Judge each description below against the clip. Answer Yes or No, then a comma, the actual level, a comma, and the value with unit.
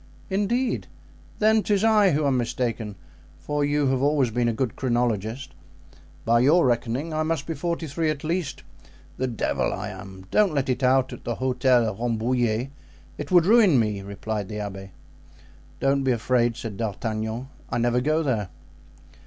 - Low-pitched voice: Yes, low, 125 Hz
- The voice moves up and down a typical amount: Yes, average, 4.9 semitones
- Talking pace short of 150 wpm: No, average, 165 wpm